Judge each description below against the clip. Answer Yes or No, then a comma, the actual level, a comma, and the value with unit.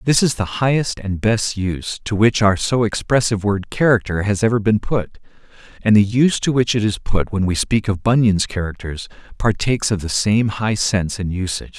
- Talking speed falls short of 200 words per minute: No, fast, 205 wpm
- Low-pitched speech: Yes, low, 105 Hz